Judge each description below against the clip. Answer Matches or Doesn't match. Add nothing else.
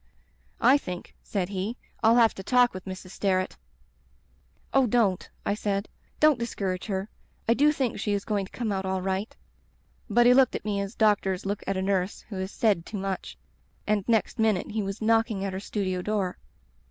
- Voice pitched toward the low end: Doesn't match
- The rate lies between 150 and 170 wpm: Doesn't match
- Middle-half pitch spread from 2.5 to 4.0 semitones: Matches